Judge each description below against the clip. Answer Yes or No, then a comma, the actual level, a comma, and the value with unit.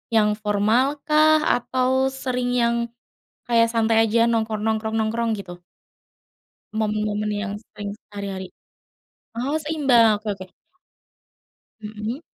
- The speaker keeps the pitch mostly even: No, average, 3.0 semitones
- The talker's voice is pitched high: Yes, high, 220 Hz